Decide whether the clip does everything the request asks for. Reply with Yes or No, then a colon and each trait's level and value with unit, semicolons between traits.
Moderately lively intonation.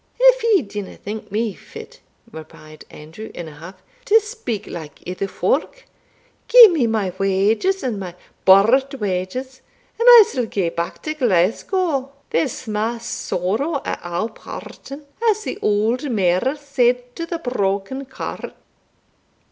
No: wide, 6.7 semitones